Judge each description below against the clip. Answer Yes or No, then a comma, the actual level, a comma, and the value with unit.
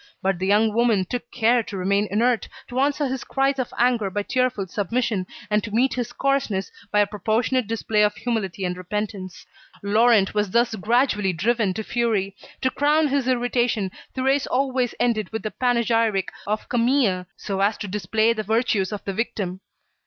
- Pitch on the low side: No, high, 220 Hz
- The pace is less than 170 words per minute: No, average, 175 wpm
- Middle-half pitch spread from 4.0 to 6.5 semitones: No, average, 3.5 semitones